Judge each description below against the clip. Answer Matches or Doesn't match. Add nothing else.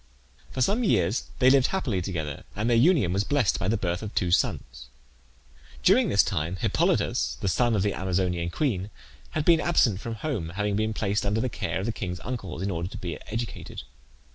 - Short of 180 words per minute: Doesn't match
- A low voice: Matches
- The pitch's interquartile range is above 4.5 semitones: Matches